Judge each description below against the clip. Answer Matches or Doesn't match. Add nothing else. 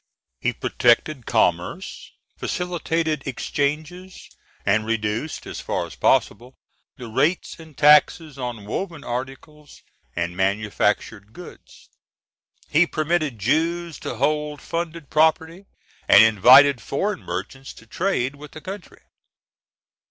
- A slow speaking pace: Matches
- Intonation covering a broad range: Matches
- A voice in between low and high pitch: Matches